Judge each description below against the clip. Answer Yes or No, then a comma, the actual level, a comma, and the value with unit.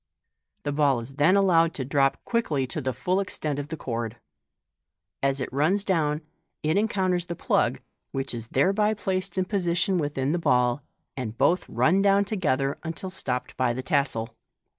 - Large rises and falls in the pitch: Yes, wide, 5.9 semitones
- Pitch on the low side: No, medium, 150 Hz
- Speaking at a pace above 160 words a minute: Yes, average, 170 wpm